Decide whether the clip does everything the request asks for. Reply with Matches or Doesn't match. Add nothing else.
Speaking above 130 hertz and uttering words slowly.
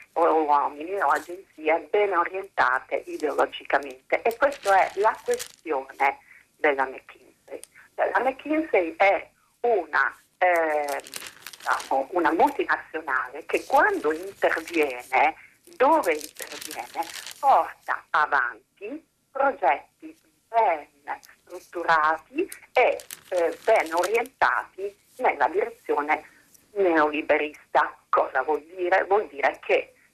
Matches